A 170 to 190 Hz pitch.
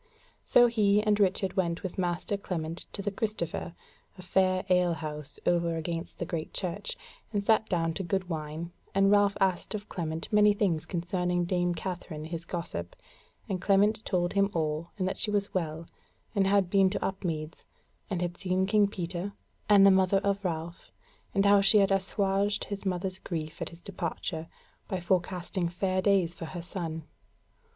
Yes: medium, 185 Hz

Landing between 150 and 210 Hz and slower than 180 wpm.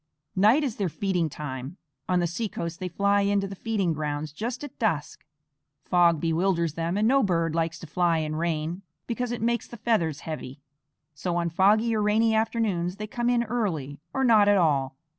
No: medium, 185 Hz; average, 195 wpm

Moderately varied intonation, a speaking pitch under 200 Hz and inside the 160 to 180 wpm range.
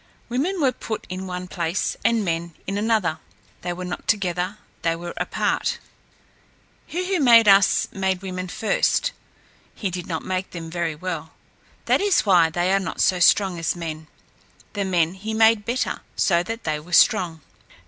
Yes: average, 3.9 semitones; medium, 185 Hz; average, 170 wpm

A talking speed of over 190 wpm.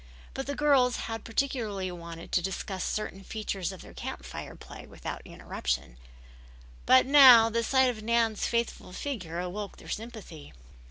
No: average, 155 wpm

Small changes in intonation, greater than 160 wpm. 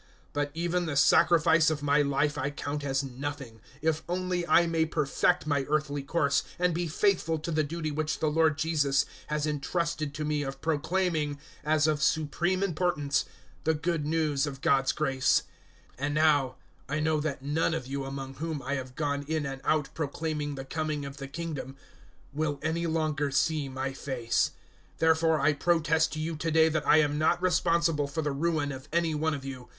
Yes: narrow, 2.2 semitones; average, 195 wpm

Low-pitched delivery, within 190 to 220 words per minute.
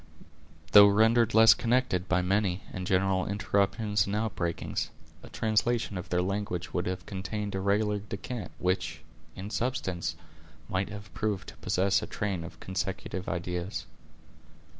No: low, 100 Hz; average, 140 wpm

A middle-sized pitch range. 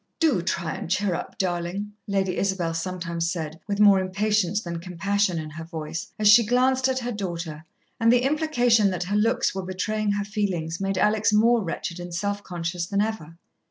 Yes: average, 3.7 semitones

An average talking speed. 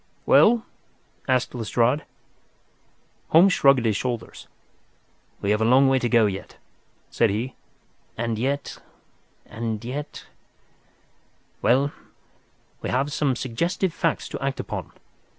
No: slow, 110 wpm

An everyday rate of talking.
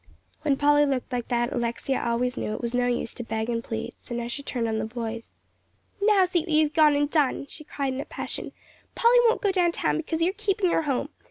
No: fast, 240 wpm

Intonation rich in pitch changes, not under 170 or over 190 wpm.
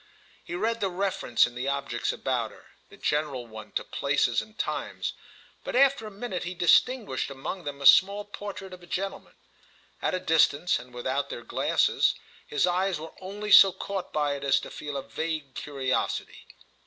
Yes: wide, 5.8 semitones; average, 180 wpm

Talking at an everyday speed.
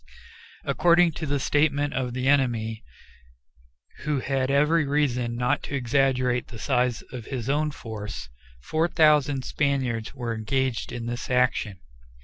No: slow, 130 wpm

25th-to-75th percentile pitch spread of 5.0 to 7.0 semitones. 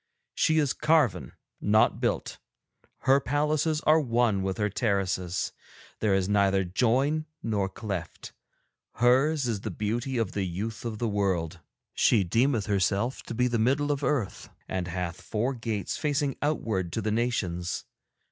Yes: wide, 5.5 semitones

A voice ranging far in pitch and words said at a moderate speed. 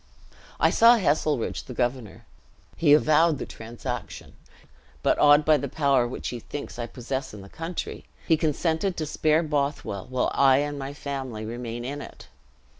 No: average, 3.8 semitones; average, 165 wpm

